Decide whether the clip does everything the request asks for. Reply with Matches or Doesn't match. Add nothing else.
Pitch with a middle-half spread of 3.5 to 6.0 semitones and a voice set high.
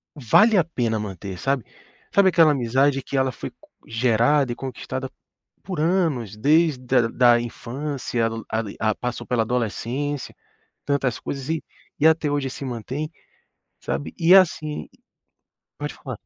Doesn't match